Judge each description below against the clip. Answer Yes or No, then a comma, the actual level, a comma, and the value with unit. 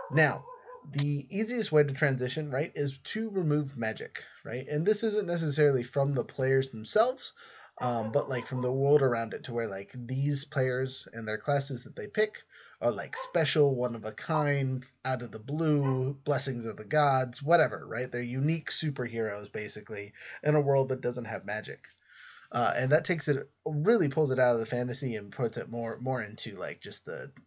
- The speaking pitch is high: No, low, 135 Hz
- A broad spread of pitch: No, average, 3.7 semitones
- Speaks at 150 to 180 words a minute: No, average, 190 wpm